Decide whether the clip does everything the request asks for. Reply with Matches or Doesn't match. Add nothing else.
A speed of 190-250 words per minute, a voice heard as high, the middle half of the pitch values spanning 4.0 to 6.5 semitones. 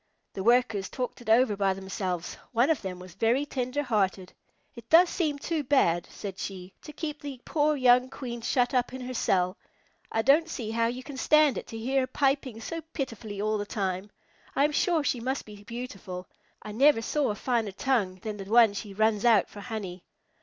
Matches